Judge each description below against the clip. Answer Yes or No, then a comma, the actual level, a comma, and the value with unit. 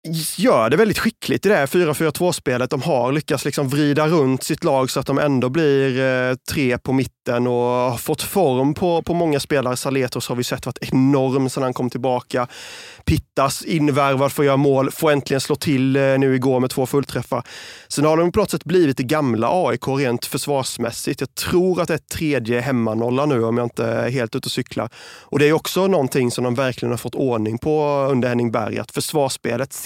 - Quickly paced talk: Yes, fast, 205 wpm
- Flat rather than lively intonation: No, average, 3.1 semitones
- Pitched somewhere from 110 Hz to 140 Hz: Yes, low, 135 Hz